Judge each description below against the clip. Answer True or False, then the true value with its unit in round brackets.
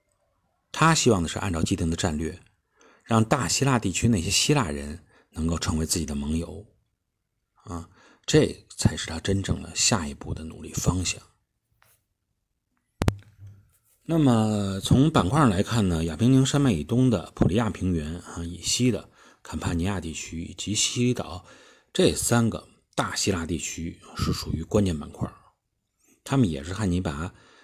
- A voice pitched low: True (100 Hz)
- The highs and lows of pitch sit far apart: False (5.0 semitones)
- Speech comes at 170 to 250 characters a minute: True (230 characters per minute)